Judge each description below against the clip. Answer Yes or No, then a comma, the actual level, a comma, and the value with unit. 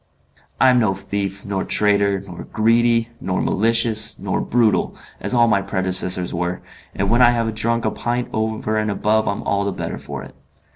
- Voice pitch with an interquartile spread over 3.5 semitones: No, average, 2.8 semitones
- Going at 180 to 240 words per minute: Yes, average, 185 wpm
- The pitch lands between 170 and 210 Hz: No, low, 105 Hz